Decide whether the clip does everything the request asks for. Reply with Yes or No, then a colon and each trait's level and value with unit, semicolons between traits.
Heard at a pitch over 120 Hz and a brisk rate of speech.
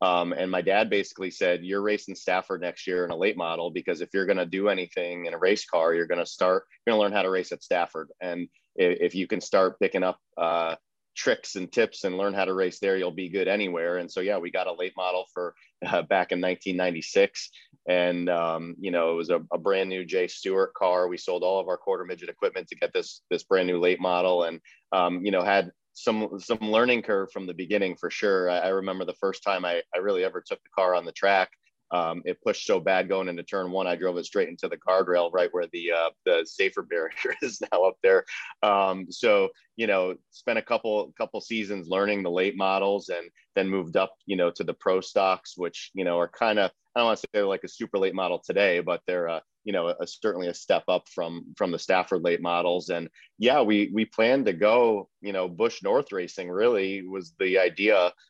No: very low, 95 Hz; fast, 240 wpm